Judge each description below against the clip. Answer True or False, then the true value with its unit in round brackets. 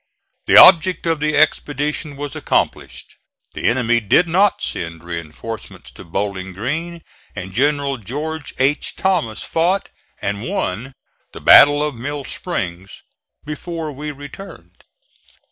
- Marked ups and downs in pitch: True (6.2 semitones)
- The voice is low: False (145 Hz)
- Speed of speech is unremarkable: False (125 wpm)